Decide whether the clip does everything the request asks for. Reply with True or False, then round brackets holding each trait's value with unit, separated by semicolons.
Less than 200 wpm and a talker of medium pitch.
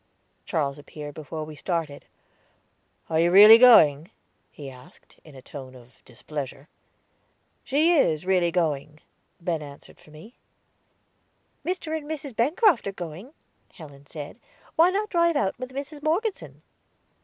True (135 wpm; 170 Hz)